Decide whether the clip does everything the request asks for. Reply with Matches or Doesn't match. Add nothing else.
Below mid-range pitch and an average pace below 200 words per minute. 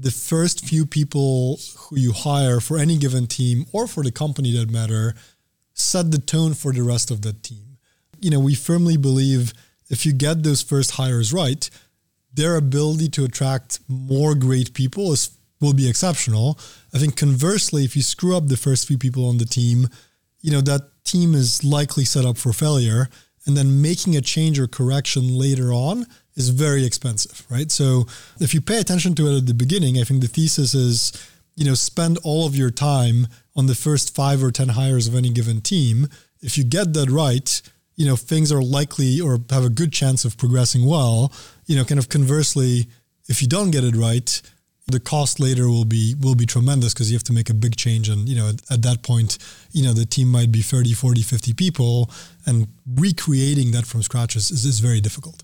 Doesn't match